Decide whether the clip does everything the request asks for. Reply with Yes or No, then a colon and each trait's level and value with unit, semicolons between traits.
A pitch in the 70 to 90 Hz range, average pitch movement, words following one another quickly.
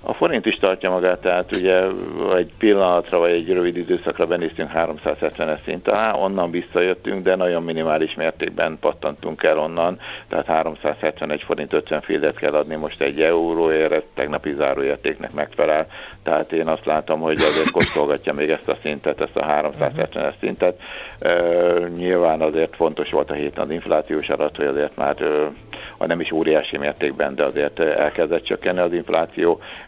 No: very low, 85 Hz; narrow, 2.1 semitones; fast, 160 wpm